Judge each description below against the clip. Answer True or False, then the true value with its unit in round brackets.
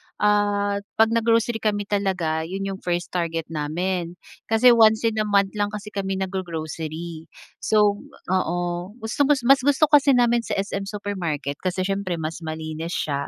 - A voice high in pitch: True (195 Hz)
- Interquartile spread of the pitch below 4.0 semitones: False (4.3 semitones)